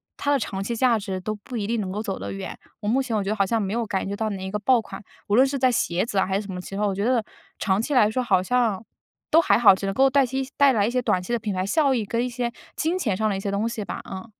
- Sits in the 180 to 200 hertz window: No, high, 215 Hz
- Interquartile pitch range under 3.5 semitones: No, average, 3.9 semitones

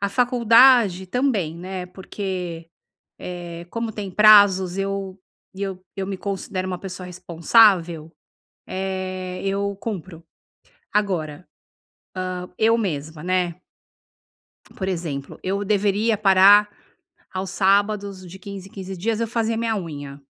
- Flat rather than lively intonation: Yes, narrow, 2.2 semitones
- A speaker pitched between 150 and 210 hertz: Yes, high, 190 Hz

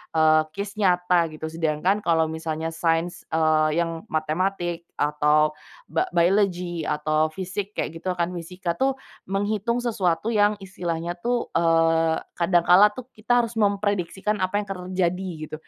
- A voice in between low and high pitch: Yes, medium, 175 Hz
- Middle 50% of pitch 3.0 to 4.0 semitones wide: Yes, average, 3.7 semitones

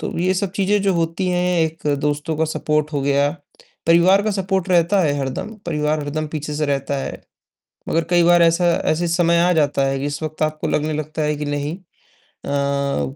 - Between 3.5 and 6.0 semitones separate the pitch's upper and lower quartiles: No, average, 3.1 semitones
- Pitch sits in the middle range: Yes, medium, 155 Hz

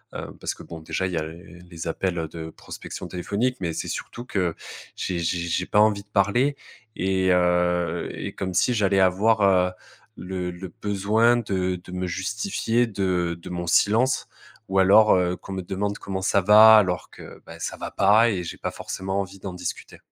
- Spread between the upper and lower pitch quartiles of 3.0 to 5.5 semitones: No, narrow, 2.6 semitones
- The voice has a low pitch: Yes, very low, 95 Hz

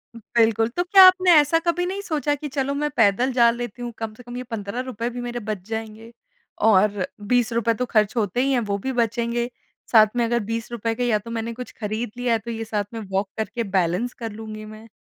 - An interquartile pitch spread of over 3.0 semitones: No, narrow, 2.4 semitones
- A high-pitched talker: Yes, high, 230 Hz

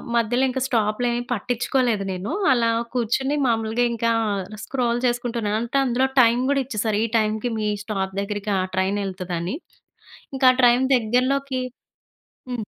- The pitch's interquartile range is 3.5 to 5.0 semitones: No, average, 2.8 semitones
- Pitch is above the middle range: Yes, high, 235 Hz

